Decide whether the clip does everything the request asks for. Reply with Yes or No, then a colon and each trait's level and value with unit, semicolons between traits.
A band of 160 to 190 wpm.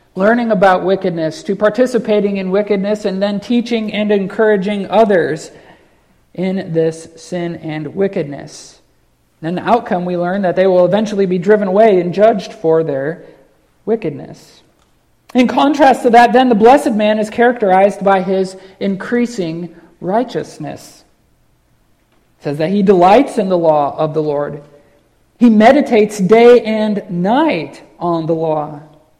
No: average, 140 wpm